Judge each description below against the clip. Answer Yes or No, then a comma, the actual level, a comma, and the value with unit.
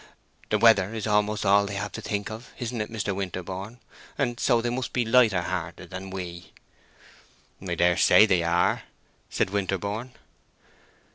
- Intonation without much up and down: No, average, 3.1 semitones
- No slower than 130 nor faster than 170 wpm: Yes, average, 160 wpm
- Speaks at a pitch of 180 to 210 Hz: No, low, 100 Hz